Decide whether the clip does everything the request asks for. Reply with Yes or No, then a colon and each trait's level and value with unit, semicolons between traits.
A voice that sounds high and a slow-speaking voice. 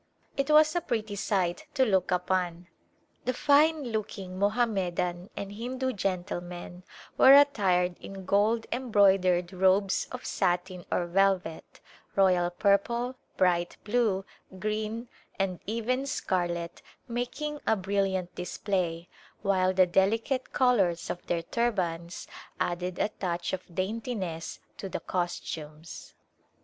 Yes: high, 195 Hz; slow, 120 wpm